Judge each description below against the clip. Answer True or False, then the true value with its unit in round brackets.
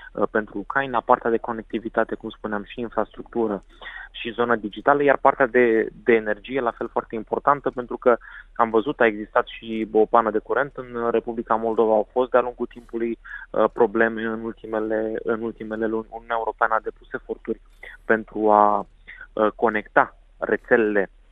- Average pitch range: False (1.6 semitones)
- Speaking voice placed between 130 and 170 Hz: False (115 Hz)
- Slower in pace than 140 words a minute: False (155 wpm)